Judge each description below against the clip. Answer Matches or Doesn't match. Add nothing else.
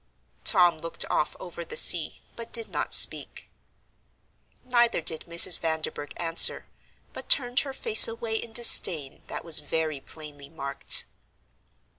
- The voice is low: Doesn't match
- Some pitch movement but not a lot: Doesn't match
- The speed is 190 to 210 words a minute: Doesn't match